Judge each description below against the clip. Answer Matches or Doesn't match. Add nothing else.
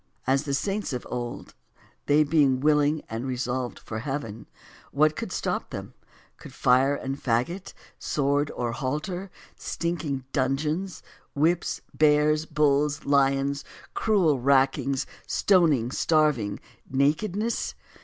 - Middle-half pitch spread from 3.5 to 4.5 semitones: Doesn't match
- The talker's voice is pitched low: Doesn't match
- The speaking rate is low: Matches